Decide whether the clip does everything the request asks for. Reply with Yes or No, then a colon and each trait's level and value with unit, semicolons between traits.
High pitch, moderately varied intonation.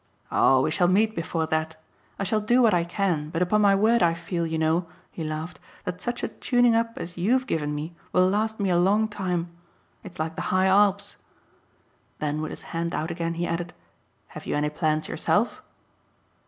No: medium, 175 Hz; average, 4.0 semitones